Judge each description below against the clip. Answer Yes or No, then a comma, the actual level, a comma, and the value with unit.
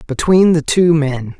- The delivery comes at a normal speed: Yes, average, 170 wpm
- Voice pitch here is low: No, medium, 155 Hz